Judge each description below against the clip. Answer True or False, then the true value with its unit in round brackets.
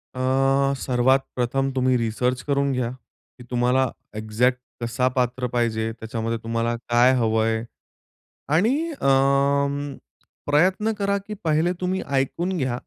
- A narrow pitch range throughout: False (3.0 semitones)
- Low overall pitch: True (130 Hz)